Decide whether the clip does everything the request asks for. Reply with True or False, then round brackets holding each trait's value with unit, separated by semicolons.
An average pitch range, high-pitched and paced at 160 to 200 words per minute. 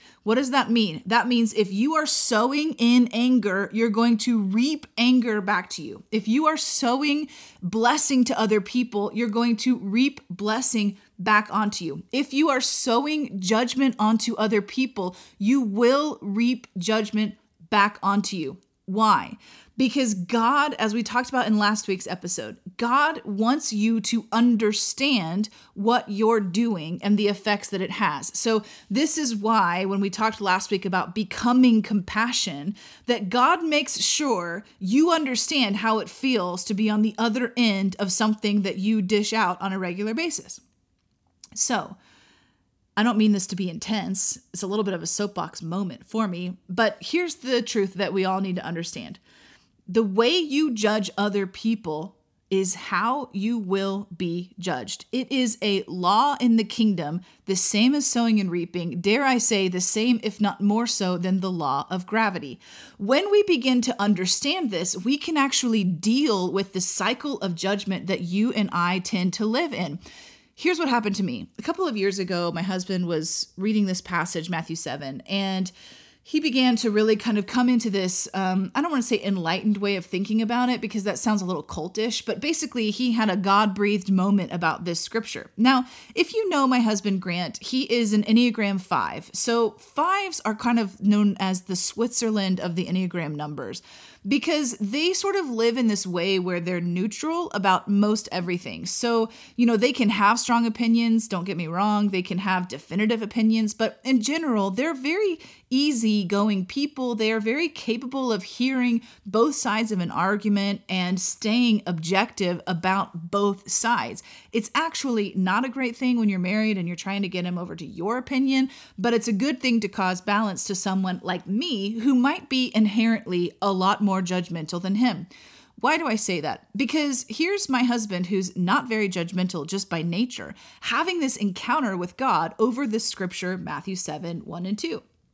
True (4.0 semitones; 215 Hz; 180 wpm)